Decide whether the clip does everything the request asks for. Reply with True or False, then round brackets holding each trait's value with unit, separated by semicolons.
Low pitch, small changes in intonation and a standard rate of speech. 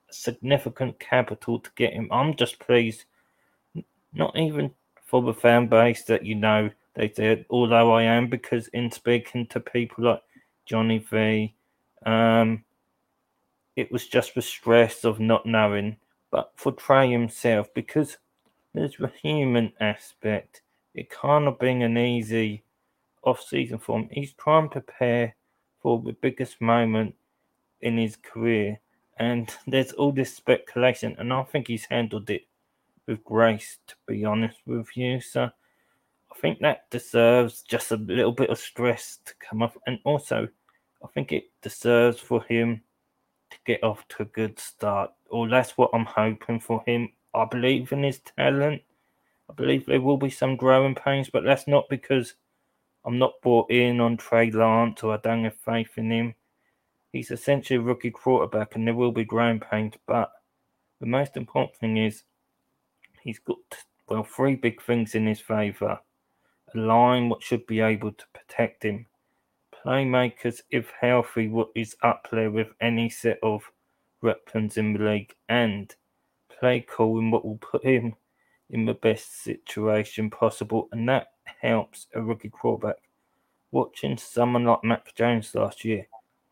True (115 Hz; 1.8 semitones; 160 wpm)